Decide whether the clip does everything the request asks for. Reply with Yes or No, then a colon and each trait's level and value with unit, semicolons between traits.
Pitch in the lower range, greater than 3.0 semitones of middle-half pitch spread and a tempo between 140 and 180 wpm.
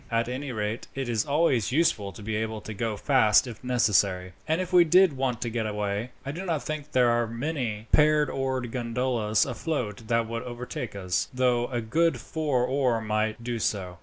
No: low, 120 Hz; average, 3.7 semitones; average, 195 wpm